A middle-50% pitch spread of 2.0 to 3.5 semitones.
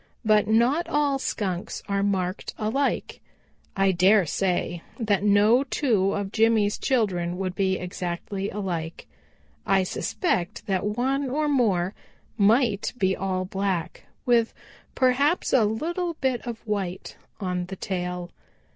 No: average, 4.5 semitones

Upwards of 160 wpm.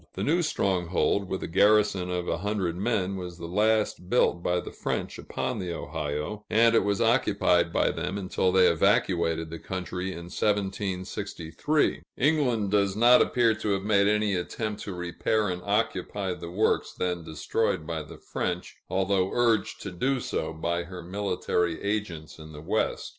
Yes: average, 170 wpm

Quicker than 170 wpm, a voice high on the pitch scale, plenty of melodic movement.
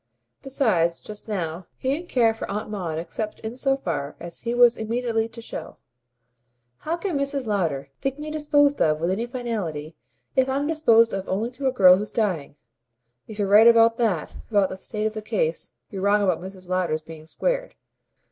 Yes: average, 190 wpm; high, 220 Hz; wide, 5.7 semitones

